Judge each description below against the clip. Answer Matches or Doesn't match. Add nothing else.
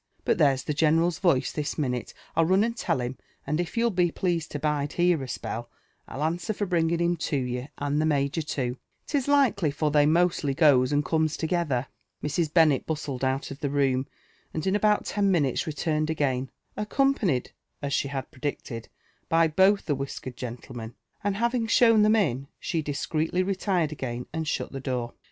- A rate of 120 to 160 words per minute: Doesn't match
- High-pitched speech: Doesn't match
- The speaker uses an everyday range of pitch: Matches